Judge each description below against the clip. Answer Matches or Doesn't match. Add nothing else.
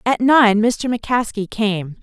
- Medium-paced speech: Matches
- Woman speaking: Matches